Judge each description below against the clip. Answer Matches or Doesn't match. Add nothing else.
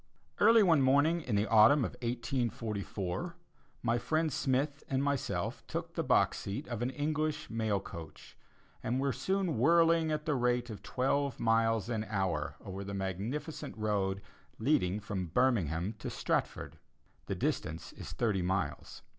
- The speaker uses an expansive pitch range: Matches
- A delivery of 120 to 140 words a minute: Doesn't match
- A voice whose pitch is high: Doesn't match